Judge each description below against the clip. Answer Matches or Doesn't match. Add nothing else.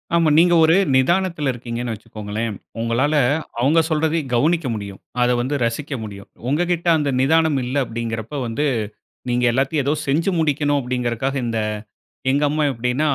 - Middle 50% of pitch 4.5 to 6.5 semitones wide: Matches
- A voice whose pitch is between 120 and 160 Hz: Matches